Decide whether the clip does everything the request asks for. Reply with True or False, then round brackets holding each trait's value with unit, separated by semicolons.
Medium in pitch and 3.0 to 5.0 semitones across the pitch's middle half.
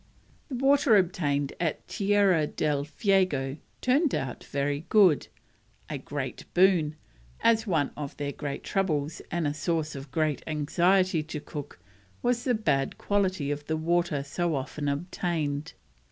True (155 Hz; 4.6 semitones)